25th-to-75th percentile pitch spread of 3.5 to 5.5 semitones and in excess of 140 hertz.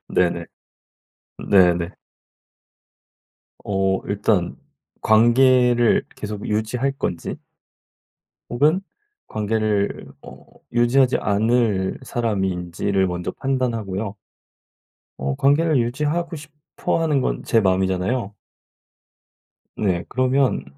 No: average, 5.1 semitones; low, 110 Hz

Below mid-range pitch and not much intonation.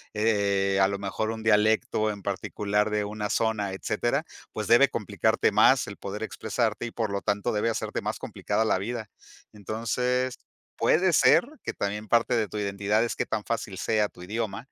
Yes: low, 105 Hz; narrow, 2.0 semitones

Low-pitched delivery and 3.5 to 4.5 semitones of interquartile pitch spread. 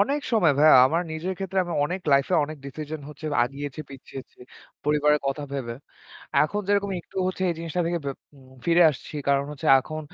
No: medium, 155 Hz; average, 3.8 semitones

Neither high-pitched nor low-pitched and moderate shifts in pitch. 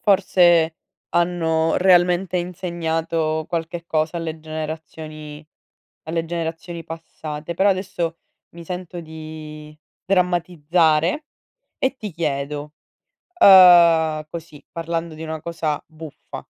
No: medium, 165 Hz; narrow, 1.9 semitones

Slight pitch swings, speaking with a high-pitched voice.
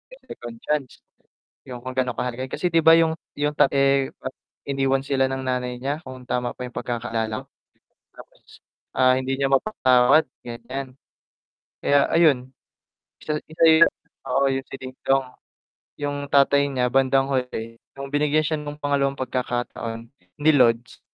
No: narrow, 2.3 semitones; low, 135 Hz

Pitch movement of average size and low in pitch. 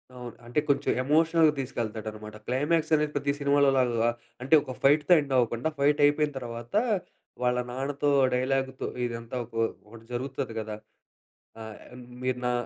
Yes: average, 3.5 semitones; low, 130 Hz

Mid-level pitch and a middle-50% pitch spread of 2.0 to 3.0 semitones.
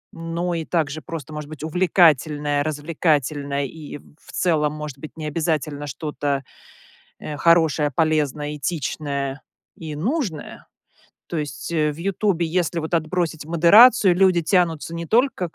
Yes: medium, 155 Hz; narrow, 2.5 semitones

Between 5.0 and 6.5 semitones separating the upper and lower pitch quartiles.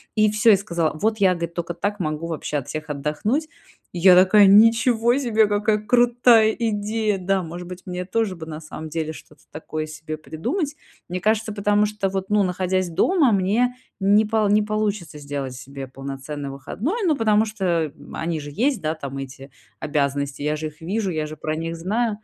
Yes: wide, 5.6 semitones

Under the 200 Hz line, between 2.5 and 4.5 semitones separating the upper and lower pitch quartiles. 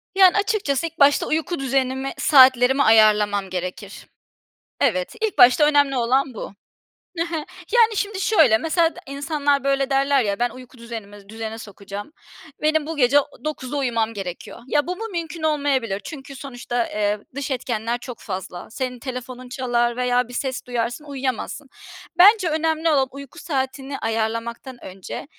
No: very high, 260 Hz; average, 4.1 semitones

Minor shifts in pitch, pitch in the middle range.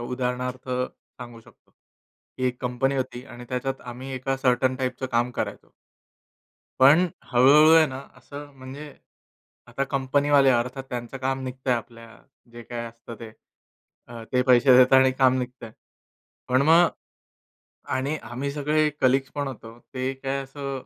No: narrow, 1.6 semitones; low, 130 Hz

